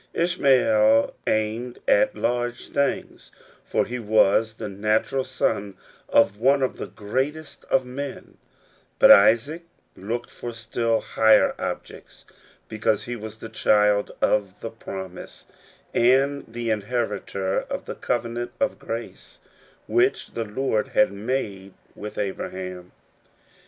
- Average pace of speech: No, slow, 120 wpm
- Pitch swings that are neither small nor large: Yes, average, 3.5 semitones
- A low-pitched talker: Yes, low, 115 Hz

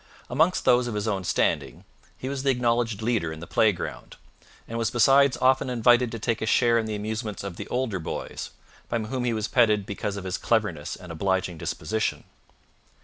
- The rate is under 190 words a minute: No, average, 195 wpm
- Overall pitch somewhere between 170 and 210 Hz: No, low, 110 Hz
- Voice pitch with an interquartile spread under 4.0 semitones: Yes, average, 3.4 semitones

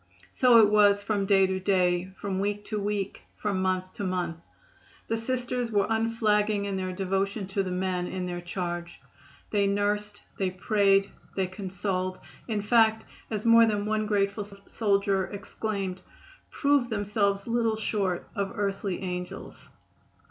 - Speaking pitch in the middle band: No, high, 200 Hz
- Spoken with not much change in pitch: Yes, narrow, 2.2 semitones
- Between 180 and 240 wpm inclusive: No, average, 150 wpm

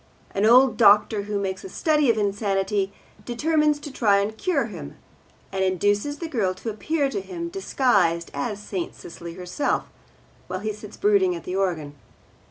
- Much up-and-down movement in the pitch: Yes, wide, 5.9 semitones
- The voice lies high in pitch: Yes, high, 205 Hz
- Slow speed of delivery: No, average, 170 wpm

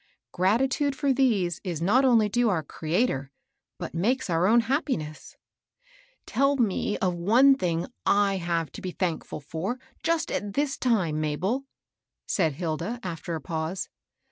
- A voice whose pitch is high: Yes, high, 195 Hz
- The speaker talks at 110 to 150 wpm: Yes, average, 145 wpm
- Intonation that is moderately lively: No, wide, 6.9 semitones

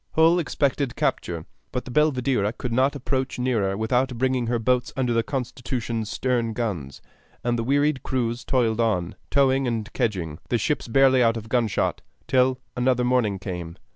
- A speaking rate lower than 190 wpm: Yes, average, 165 wpm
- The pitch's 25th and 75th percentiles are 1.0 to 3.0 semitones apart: Yes, average, 2.7 semitones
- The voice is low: Yes, low, 125 Hz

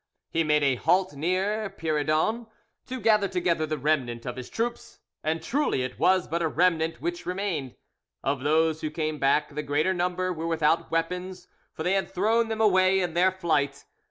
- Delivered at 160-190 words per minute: Yes, average, 185 wpm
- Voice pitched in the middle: Yes, medium, 170 Hz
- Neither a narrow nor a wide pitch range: Yes, average, 3.6 semitones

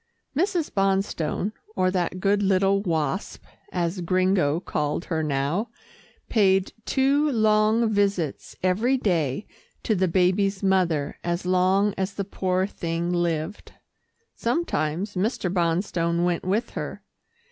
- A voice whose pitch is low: No, medium, 185 Hz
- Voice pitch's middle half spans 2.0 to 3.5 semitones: Yes, average, 3.1 semitones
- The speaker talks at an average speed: No, slow, 120 wpm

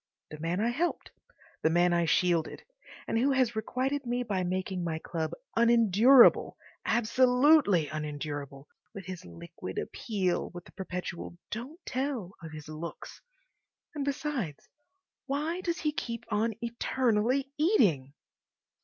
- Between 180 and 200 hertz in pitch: No, high, 215 Hz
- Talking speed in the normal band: No, slow, 130 wpm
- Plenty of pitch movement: Yes, wide, 7.3 semitones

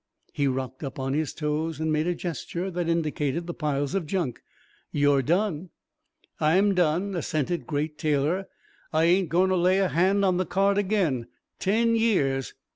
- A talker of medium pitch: Yes, medium, 165 Hz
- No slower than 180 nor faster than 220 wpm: No, average, 170 wpm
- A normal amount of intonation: Yes, average, 4.0 semitones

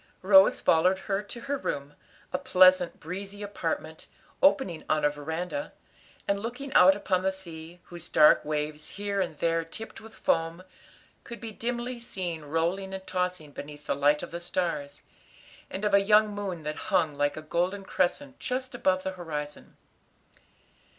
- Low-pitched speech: No, medium, 185 Hz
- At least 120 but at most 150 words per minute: No, average, 165 wpm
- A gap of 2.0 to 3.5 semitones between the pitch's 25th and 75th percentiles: No, average, 4.1 semitones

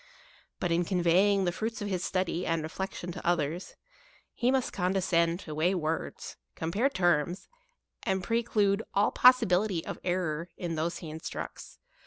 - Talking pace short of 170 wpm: Yes, average, 150 wpm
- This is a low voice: No, medium, 180 Hz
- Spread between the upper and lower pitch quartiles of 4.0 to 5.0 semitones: No, average, 2.9 semitones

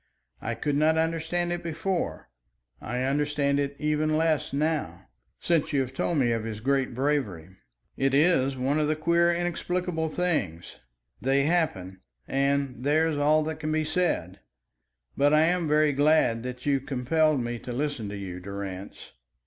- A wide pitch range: No, average, 4.0 semitones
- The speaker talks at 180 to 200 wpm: No, average, 160 wpm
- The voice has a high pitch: No, medium, 145 Hz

